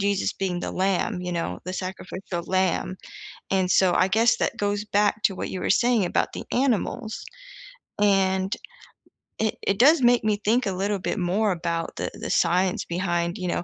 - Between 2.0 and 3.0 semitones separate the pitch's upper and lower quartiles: Yes, narrow, 2.5 semitones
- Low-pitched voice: No, high, 195 Hz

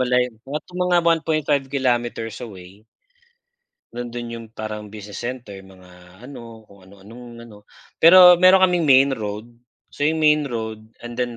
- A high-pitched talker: No, low, 120 Hz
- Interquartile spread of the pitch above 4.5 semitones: Yes, average, 5.2 semitones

